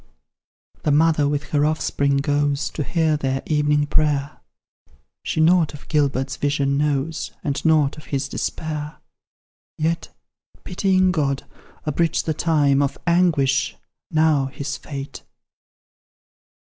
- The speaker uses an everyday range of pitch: No, narrow, 2.1 semitones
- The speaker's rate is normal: No, slow, 120 wpm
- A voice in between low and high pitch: Yes, medium, 150 Hz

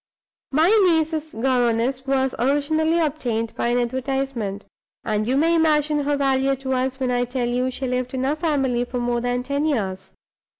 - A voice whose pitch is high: Yes, very high, 265 Hz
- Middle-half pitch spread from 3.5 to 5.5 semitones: No, average, 3.0 semitones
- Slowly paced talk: No, average, 175 wpm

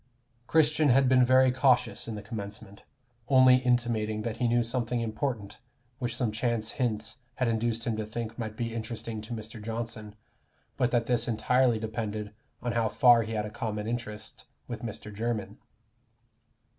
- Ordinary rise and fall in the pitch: No, narrow, 2.1 semitones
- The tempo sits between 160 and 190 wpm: Yes, average, 165 wpm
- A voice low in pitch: Yes, low, 115 Hz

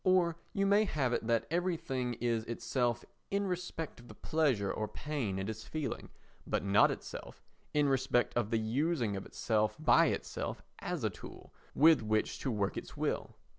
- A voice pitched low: Yes, low, 125 Hz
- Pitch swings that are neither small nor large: No, wide, 6.5 semitones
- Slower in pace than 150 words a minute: No, average, 175 wpm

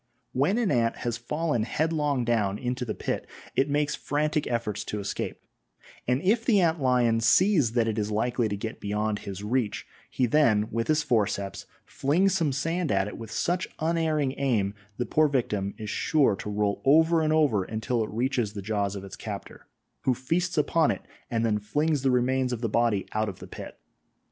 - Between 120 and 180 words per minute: No, average, 195 wpm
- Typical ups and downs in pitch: No, wide, 5.9 semitones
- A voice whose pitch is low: Yes, low, 125 Hz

